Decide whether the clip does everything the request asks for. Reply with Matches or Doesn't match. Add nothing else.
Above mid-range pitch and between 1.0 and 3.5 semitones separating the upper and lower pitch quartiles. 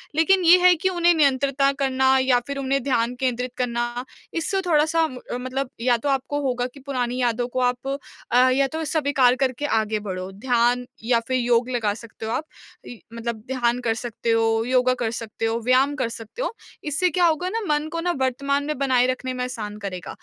Matches